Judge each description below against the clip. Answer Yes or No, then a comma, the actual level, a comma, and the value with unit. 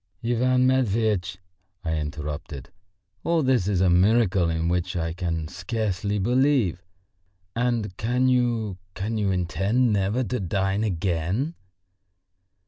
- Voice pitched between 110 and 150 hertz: No, low, 100 Hz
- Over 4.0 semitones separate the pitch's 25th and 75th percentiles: Yes, average, 5.1 semitones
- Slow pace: Yes, slow, 120 wpm